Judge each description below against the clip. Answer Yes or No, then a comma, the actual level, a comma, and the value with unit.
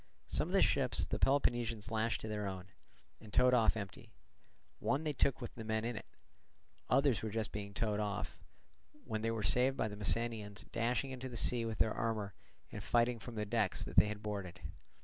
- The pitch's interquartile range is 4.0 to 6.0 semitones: No, narrow, 2.4 semitones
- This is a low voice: Yes, low, 110 Hz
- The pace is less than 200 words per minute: No, fast, 205 wpm